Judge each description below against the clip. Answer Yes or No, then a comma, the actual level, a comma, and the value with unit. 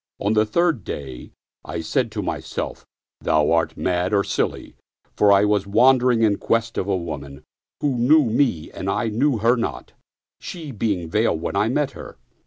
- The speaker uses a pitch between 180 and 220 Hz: No, low, 105 Hz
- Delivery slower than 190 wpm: No, average, 195 wpm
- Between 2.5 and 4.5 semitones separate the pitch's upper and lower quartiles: No, average, 5.1 semitones